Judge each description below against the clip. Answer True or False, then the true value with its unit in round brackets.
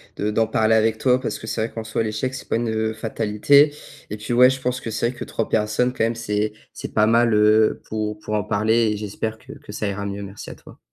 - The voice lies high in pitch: False (110 Hz)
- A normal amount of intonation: False (1.6 semitones)